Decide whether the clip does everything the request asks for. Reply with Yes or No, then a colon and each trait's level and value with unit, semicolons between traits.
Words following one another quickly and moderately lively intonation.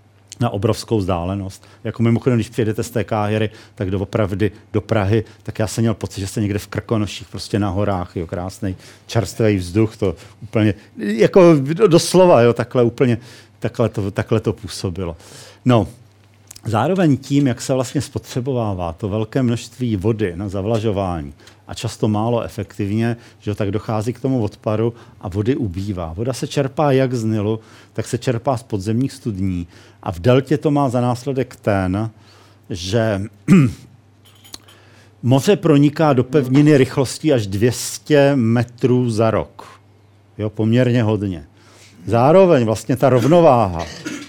No: average, 145 wpm; average, 3.3 semitones